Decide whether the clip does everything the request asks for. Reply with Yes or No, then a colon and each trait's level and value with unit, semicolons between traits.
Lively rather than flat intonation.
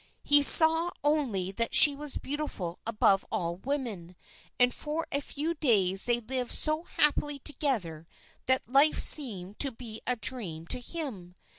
Yes: wide, 7.1 semitones